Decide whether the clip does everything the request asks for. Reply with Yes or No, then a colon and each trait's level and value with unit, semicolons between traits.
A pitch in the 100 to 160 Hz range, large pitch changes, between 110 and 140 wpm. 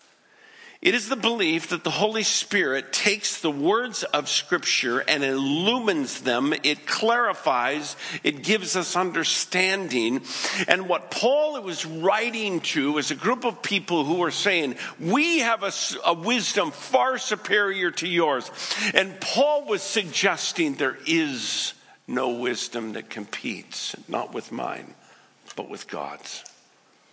No: high, 200 Hz; wide, 6.5 semitones; slow, 135 wpm